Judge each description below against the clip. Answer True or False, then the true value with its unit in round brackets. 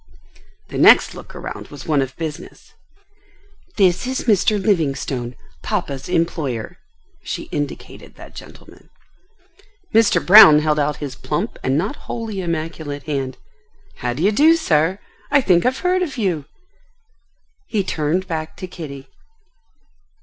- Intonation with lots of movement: True (5.9 semitones)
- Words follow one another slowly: True (130 wpm)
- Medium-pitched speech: True (165 Hz)